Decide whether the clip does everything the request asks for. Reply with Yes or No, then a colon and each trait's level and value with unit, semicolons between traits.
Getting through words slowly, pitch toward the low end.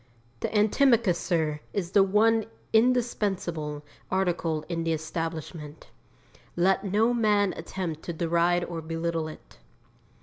No: slow, 110 wpm; medium, 175 Hz